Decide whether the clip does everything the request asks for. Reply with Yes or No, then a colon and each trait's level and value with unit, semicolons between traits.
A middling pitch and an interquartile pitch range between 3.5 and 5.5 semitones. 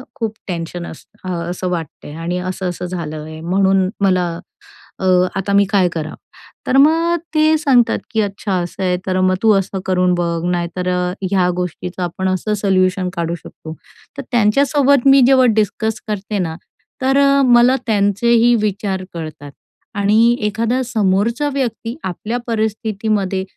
No: high, 195 Hz; average, 4.2 semitones